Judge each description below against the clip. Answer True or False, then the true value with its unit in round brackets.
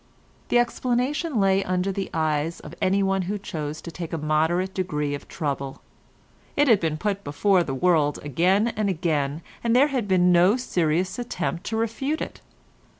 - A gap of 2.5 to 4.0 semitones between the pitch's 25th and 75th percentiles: False (5.0 semitones)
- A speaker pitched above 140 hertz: True (185 Hz)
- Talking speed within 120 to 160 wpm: False (170 wpm)